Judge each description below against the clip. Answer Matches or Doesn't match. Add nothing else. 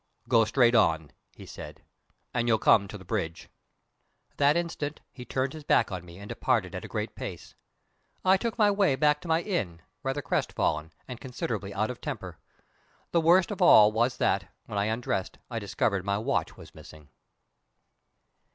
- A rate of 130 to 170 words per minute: Doesn't match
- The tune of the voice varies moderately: Doesn't match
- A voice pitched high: Doesn't match